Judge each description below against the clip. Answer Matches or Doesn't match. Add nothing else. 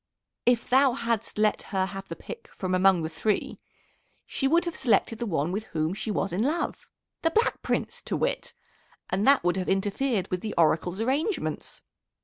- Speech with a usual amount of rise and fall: Doesn't match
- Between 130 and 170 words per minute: Doesn't match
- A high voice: Matches